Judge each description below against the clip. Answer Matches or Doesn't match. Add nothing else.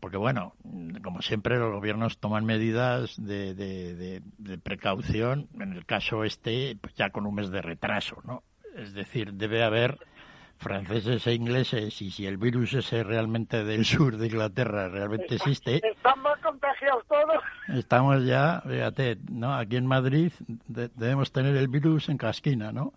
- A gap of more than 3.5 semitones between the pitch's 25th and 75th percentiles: Matches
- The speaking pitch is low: Matches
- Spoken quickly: Doesn't match